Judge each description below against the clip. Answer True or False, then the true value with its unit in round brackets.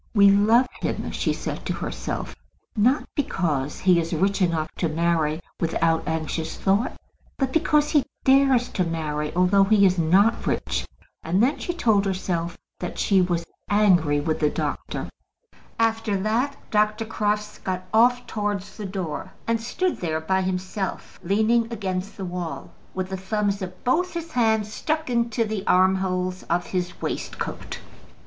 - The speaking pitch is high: True (195 Hz)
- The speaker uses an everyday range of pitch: True (4.1 semitones)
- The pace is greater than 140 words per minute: True (155 wpm)